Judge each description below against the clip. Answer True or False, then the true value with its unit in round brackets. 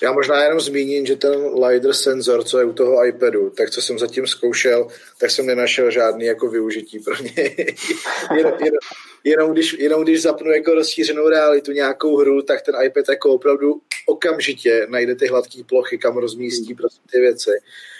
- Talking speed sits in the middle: False (175 wpm)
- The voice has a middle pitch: True (155 Hz)